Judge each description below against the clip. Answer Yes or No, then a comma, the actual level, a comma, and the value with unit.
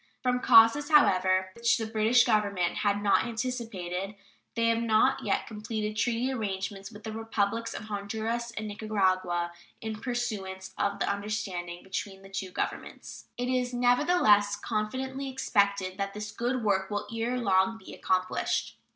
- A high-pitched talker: Yes, high, 215 Hz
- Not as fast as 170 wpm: Yes, average, 150 wpm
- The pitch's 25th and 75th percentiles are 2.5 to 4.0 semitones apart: Yes, average, 3.1 semitones